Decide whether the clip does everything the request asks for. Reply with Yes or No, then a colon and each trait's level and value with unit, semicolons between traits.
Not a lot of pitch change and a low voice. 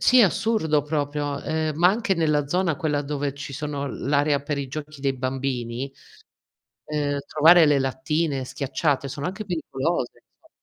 No: narrow, 2.3 semitones; medium, 145 Hz